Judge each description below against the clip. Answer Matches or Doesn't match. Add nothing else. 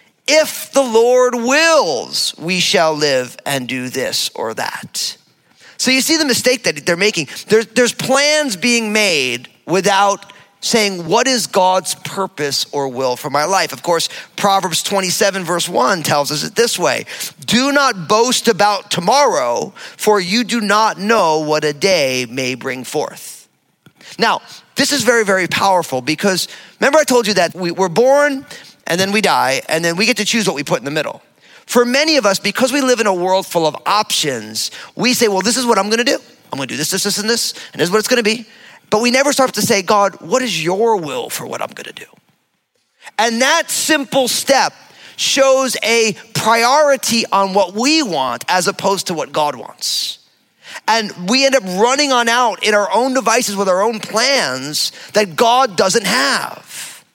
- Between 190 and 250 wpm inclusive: Matches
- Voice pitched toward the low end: Doesn't match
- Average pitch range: Doesn't match